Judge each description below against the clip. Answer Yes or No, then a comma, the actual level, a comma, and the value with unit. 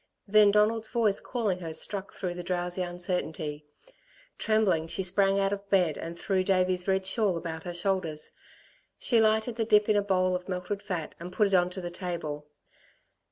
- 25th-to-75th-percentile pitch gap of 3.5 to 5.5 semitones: No, narrow, 2.6 semitones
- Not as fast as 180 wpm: No, average, 185 wpm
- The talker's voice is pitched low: No, medium, 185 Hz